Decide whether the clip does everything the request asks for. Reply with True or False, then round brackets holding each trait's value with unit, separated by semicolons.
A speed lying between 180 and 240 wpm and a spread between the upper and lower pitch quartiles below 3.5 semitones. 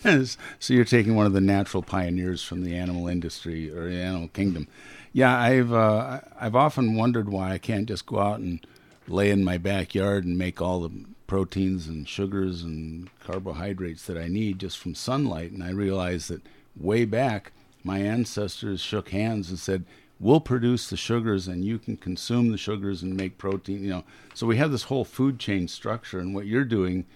False (195 wpm; 3.8 semitones)